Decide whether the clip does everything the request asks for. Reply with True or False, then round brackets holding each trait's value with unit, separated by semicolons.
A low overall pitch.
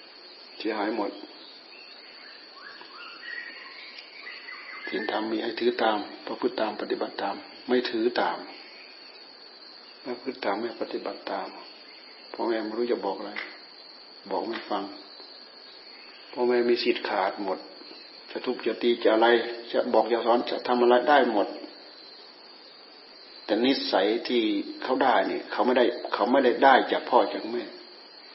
False (310 Hz)